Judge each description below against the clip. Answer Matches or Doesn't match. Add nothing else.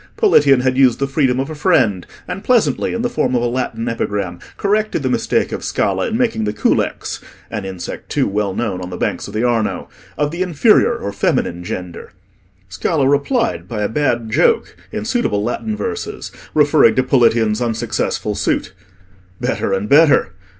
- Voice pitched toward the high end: Doesn't match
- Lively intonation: Matches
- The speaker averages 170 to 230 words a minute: Matches